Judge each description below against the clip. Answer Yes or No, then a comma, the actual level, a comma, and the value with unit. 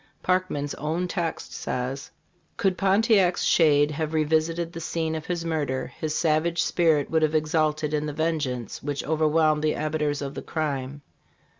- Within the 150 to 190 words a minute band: Yes, average, 155 wpm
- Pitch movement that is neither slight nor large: No, narrow, 2.0 semitones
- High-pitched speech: No, medium, 155 Hz